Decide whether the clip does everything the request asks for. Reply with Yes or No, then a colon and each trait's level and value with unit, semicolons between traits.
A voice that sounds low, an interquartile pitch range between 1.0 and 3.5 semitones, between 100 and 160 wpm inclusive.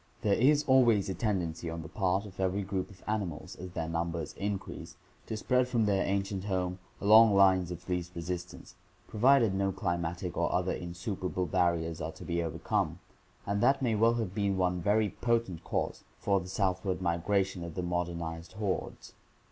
No: very low, 95 Hz; average, 2.9 semitones; average, 180 wpm